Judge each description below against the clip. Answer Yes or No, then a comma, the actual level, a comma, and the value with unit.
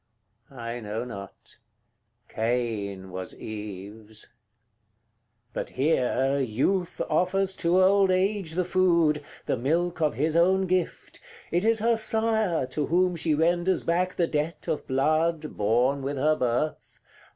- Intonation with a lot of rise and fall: Yes, wide, 6.8 semitones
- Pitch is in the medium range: Yes, medium, 155 Hz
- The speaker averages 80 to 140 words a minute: Yes, slow, 135 wpm